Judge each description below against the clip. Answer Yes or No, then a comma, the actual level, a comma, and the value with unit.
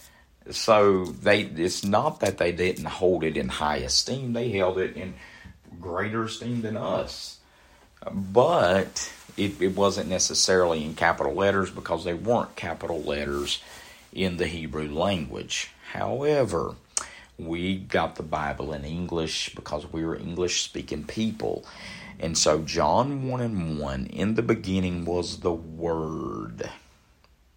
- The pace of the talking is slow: Yes, slow, 130 wpm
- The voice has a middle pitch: No, very low, 90 Hz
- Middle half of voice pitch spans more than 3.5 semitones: Yes, average, 4.0 semitones